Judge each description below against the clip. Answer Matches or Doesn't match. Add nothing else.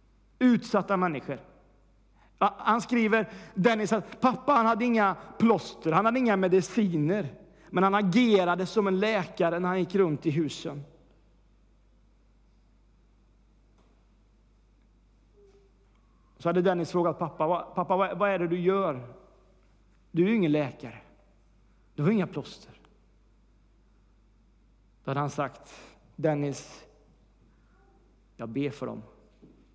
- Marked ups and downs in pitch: Matches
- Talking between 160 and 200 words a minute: Doesn't match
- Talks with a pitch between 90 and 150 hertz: Doesn't match